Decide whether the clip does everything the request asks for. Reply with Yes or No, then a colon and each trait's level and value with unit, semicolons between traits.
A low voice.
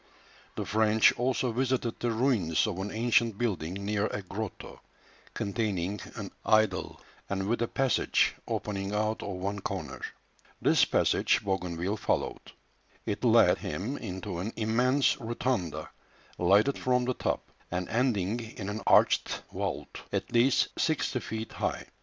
Yes: low, 110 Hz